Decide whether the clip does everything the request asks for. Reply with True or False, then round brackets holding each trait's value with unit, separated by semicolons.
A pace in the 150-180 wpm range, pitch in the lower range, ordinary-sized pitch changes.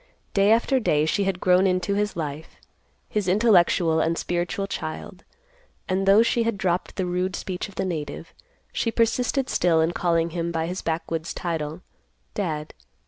False (160 wpm; 180 Hz; 3.3 semitones)